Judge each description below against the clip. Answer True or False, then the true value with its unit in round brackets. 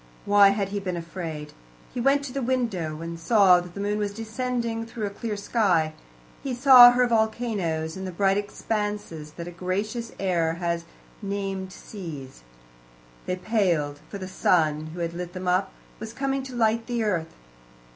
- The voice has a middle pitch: False (200 Hz)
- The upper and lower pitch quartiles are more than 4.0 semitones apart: True (4.9 semitones)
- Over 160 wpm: True (175 wpm)